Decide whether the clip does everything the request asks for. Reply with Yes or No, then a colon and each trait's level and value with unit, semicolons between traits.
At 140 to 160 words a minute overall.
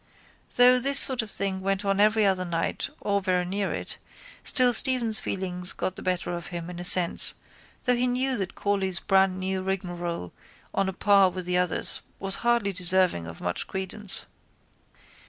No: average, 175 wpm